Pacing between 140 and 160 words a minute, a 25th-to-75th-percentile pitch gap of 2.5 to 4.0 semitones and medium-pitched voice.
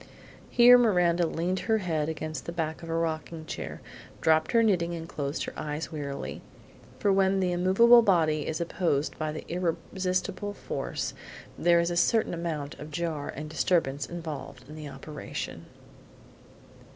Yes: average, 155 wpm; average, 2.9 semitones; medium, 165 Hz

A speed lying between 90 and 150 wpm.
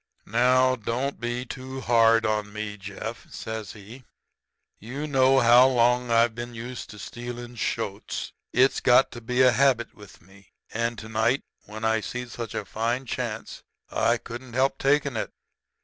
No: average, 165 wpm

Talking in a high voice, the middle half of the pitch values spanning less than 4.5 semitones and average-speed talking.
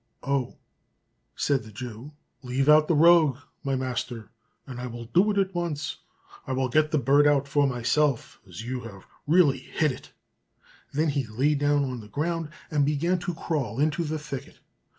No: medium, 140 Hz; average, 3.3 semitones; average, 180 wpm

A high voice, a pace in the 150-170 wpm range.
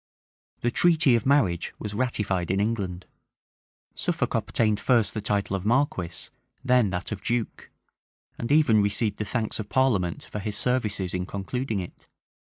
No: low, 105 Hz; average, 155 wpm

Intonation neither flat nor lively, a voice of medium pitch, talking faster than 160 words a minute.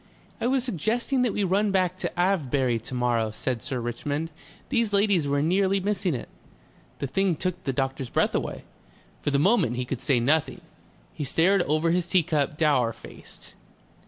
No: wide, 6.5 semitones; medium, 160 Hz; average, 180 wpm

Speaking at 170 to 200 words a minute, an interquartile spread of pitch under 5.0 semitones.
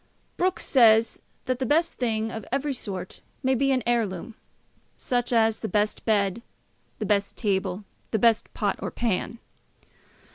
No: average, 150 wpm; average, 3.2 semitones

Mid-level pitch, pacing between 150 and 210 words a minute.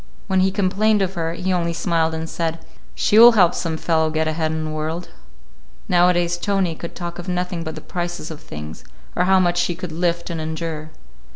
Yes: medium, 170 Hz; fast, 205 wpm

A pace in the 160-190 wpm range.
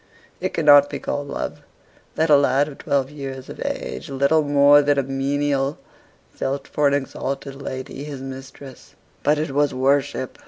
Yes: average, 165 wpm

